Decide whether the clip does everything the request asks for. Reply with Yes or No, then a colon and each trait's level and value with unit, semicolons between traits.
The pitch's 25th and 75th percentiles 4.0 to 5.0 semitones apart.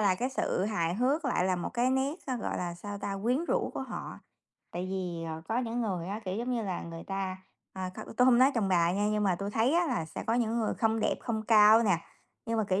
Yes: average, 4.4 semitones